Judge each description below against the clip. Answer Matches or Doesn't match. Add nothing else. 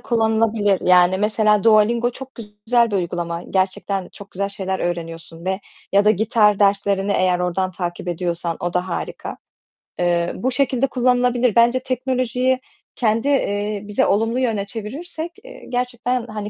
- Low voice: Doesn't match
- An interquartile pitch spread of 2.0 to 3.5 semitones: Doesn't match